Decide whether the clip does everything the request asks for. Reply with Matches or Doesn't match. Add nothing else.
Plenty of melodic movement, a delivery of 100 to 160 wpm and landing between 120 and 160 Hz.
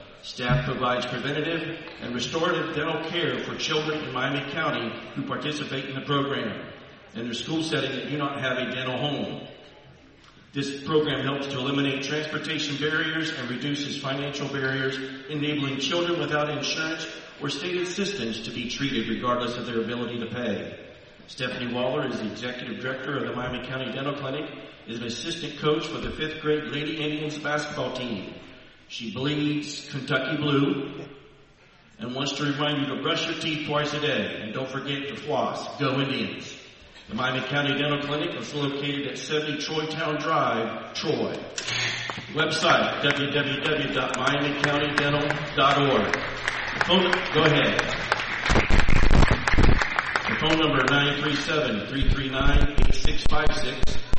Doesn't match